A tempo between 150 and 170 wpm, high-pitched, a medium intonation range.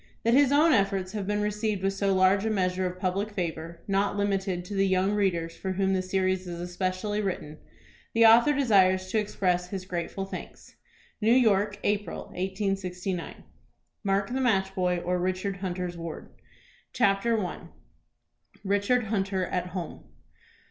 No: average, 155 wpm; high, 195 Hz; narrow, 2.1 semitones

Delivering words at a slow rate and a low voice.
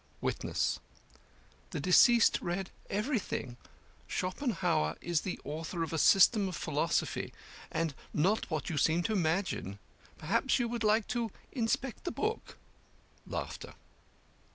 No: slow, 125 wpm; medium, 185 Hz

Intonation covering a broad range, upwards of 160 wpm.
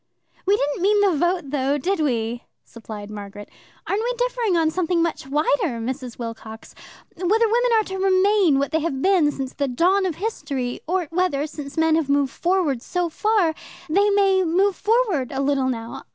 Yes: wide, 6.1 semitones; average, 185 wpm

